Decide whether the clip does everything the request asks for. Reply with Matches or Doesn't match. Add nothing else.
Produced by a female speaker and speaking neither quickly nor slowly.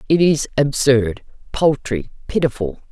Doesn't match